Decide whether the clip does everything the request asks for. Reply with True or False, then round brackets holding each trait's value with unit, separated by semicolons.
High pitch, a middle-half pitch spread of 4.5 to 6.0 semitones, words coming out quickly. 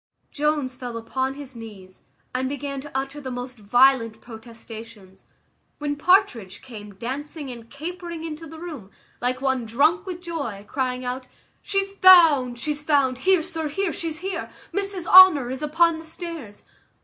False (275 Hz; 5.1 semitones; 155 wpm)